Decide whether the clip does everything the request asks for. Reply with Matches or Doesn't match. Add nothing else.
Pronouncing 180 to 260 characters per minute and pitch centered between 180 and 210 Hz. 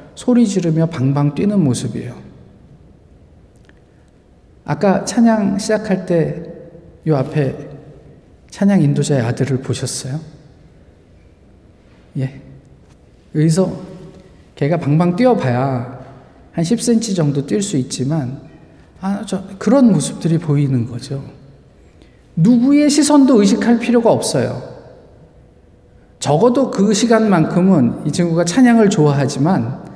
Doesn't match